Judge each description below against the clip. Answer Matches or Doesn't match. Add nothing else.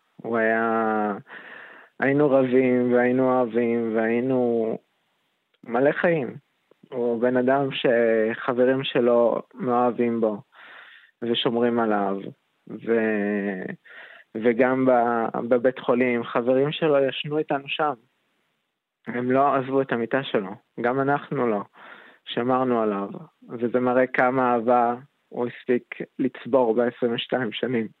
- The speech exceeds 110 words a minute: Doesn't match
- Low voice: Matches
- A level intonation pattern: Matches